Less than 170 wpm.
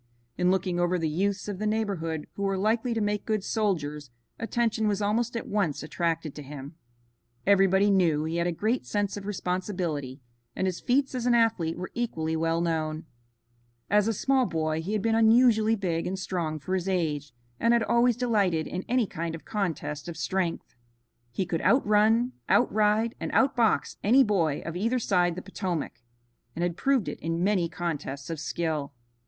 No: average, 180 wpm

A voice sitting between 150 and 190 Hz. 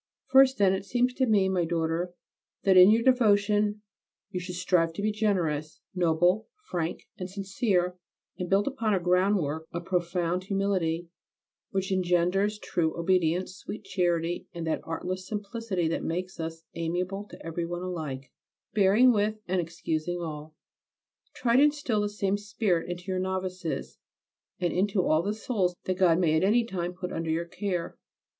Yes: medium, 185 Hz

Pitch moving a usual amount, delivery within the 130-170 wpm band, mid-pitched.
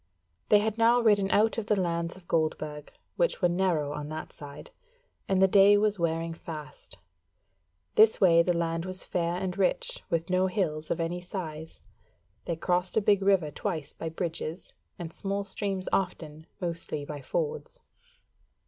Yes: average, 3.5 semitones; average, 165 wpm; medium, 180 Hz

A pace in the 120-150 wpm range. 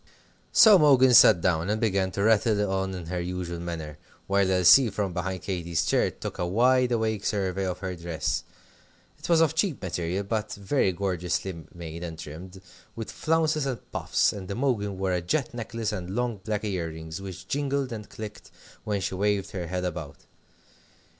No: average, 180 wpm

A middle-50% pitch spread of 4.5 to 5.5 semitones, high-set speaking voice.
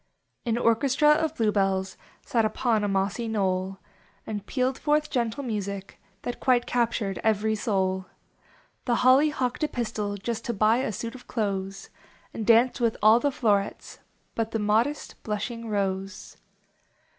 No: average, 3.3 semitones; high, 225 Hz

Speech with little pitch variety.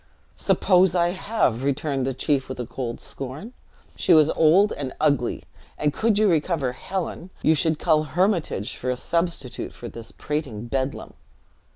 No: average, 4.9 semitones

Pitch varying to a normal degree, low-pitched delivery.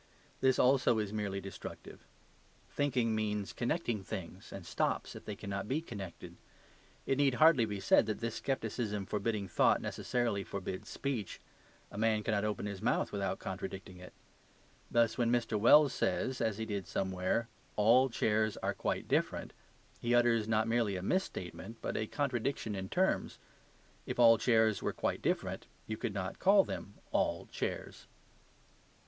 Yes: average, 3.2 semitones; low, 110 Hz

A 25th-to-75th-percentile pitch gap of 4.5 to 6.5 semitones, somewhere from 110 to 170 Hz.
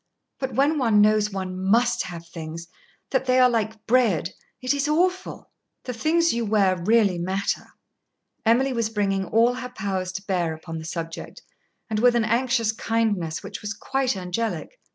No: average, 4.9 semitones; high, 220 Hz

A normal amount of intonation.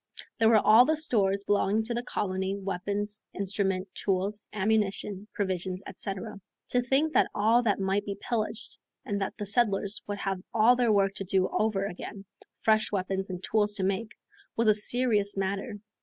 No: narrow, 2.2 semitones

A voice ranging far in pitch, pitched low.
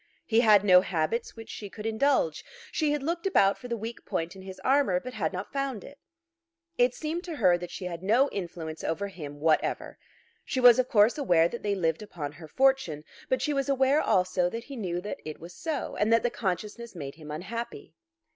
No: wide, 6.5 semitones; high, 210 Hz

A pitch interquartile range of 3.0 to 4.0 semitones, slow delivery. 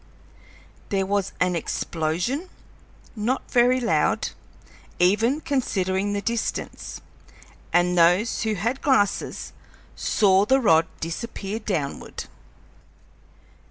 No: average, 4.6 semitones; slow, 90 wpm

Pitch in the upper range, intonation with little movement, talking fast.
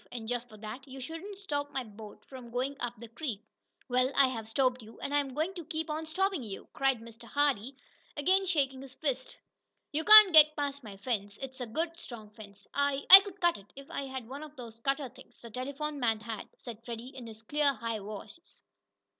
No: very high, 265 Hz; average, 4.4 semitones; fast, 215 wpm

